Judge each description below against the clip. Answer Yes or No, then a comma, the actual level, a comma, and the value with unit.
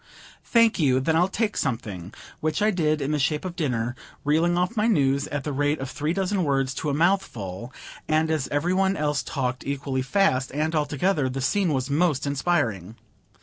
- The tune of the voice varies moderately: Yes, average, 4.6 semitones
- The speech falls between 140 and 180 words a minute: No, average, 195 wpm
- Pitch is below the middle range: No, medium, 150 Hz